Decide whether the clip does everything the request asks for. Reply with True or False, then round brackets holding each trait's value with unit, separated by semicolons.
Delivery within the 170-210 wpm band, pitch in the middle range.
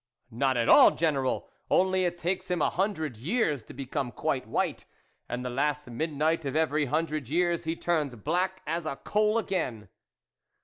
True (175 wpm; 155 Hz)